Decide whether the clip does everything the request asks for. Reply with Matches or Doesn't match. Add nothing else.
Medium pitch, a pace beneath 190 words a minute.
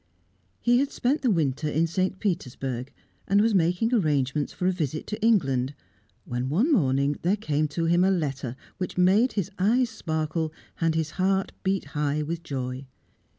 Matches